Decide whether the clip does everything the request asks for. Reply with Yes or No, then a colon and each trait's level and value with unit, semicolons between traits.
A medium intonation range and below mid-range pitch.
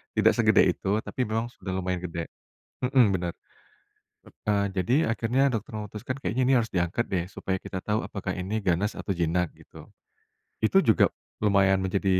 Yes: average, 3.5 semitones; low, 100 Hz